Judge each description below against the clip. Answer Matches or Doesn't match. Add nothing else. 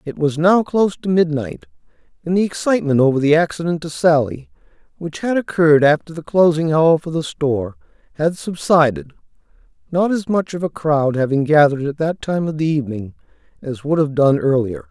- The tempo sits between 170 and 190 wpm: Matches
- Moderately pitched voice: Matches